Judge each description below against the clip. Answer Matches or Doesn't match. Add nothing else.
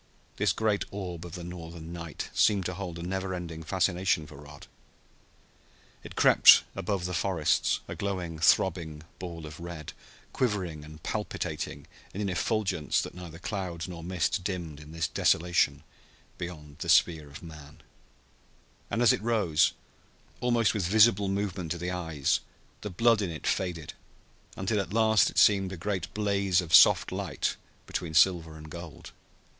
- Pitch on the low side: Matches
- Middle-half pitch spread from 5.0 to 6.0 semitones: Doesn't match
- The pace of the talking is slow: Doesn't match